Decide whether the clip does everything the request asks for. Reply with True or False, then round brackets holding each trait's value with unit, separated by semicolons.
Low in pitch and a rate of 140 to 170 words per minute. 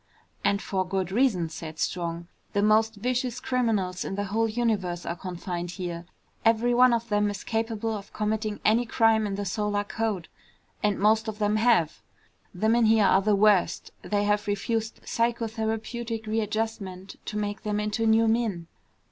False (210 Hz; 165 wpm)